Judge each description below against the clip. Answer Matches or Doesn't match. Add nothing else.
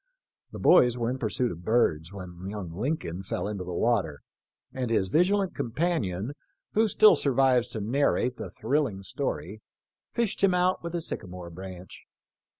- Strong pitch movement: Matches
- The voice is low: Matches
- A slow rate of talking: Doesn't match